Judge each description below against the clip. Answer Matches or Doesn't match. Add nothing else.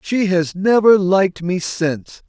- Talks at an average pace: Matches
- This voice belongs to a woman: Doesn't match